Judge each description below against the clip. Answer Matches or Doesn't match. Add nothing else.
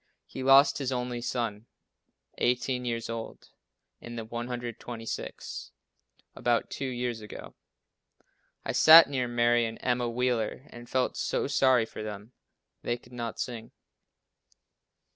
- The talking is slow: Matches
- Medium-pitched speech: Doesn't match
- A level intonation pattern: Matches